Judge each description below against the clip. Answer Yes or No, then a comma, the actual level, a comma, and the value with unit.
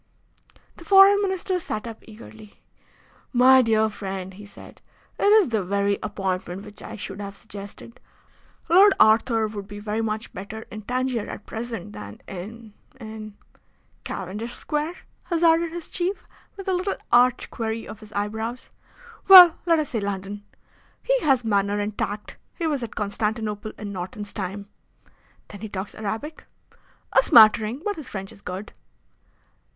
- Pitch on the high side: Yes, high, 220 Hz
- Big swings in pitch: No, average, 4.4 semitones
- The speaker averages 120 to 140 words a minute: No, average, 155 wpm